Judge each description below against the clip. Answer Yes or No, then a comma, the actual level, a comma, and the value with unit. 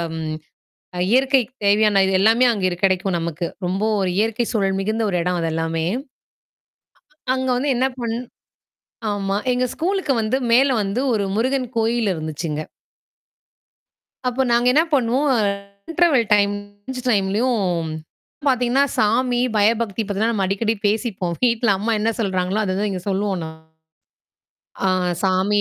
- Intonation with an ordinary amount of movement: Yes, average, 4.2 semitones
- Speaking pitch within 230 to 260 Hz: No, high, 215 Hz